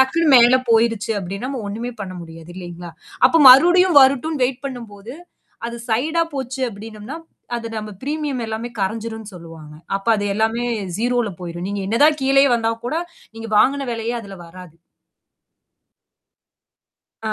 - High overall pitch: Yes, high, 230 Hz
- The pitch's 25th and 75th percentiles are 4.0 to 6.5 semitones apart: Yes, average, 4.6 semitones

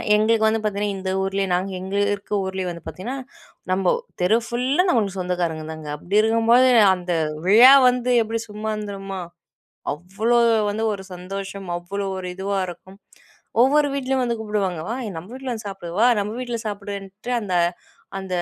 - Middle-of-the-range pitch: No, high, 200 Hz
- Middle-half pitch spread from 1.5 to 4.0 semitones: Yes, average, 3.3 semitones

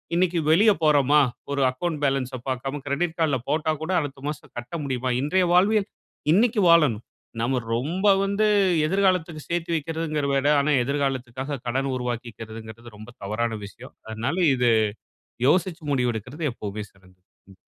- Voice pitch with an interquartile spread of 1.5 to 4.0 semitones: No, average, 5.3 semitones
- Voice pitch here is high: No, medium, 140 Hz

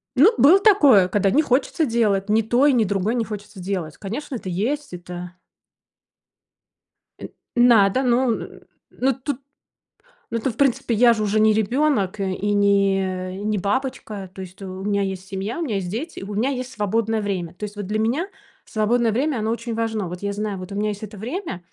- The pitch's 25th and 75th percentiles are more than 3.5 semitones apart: Yes, average, 3.9 semitones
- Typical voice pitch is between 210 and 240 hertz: Yes, high, 215 Hz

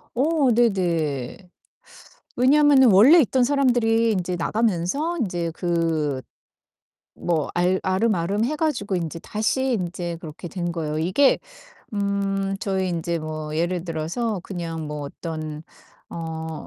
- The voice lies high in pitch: No, medium, 180 Hz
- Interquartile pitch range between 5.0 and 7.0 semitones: Yes, wide, 5.6 semitones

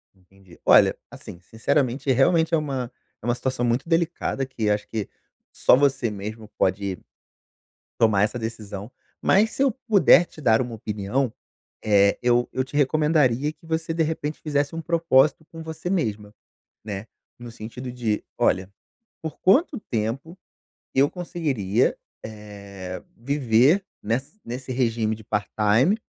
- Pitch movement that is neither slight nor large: No, wide, 6.2 semitones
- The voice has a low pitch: Yes, low, 125 Hz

